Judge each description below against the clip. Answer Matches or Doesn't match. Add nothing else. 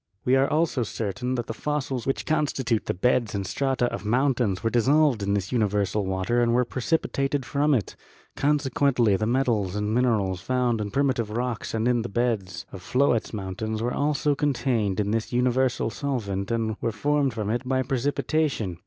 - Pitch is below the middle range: Matches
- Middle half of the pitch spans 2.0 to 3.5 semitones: Doesn't match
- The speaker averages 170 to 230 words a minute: Matches